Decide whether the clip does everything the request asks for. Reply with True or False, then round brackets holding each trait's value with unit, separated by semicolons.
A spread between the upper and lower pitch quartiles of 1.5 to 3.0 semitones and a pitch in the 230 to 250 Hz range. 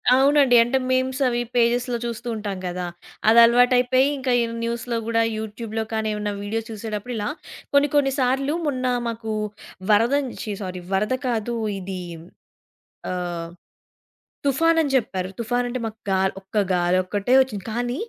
False (3.5 semitones; 235 Hz)